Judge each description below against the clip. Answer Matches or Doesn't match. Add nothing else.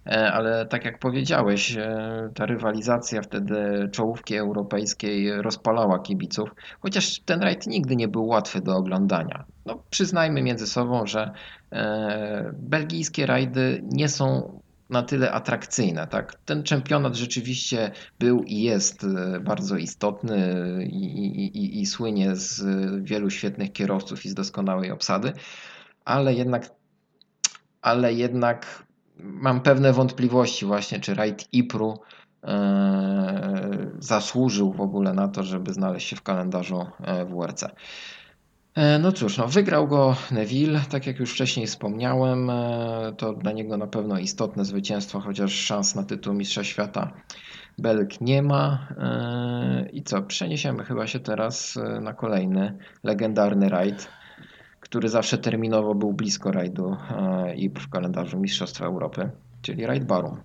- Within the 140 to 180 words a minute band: Doesn't match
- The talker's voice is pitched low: Matches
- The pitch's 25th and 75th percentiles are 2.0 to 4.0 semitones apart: Doesn't match